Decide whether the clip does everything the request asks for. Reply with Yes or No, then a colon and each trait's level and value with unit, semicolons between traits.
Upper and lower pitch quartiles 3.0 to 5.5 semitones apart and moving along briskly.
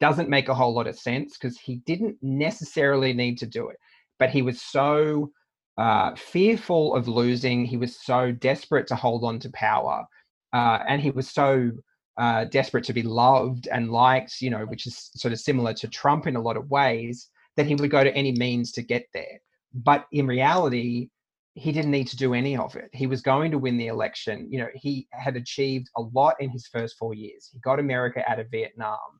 No: narrow, 2.4 semitones; fast, 215 wpm